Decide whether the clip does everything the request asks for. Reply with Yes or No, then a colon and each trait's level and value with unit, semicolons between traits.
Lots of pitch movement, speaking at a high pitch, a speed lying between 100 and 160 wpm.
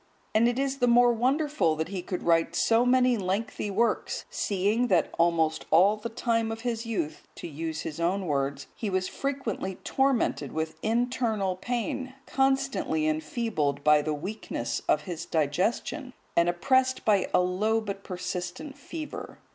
Yes: wide, 6.4 semitones; high, 205 Hz; average, 155 wpm